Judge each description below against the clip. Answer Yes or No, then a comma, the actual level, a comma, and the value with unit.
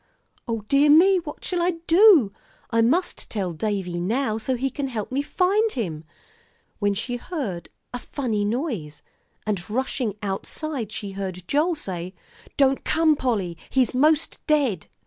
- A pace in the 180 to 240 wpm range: No, average, 155 wpm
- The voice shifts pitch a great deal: Yes, wide, 7.0 semitones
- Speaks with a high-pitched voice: Yes, high, 245 Hz